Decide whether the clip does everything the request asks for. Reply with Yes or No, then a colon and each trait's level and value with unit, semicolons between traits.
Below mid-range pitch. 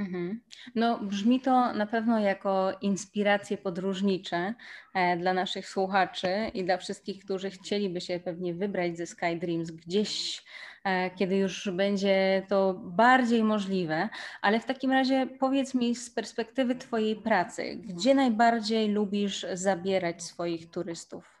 No: high, 200 Hz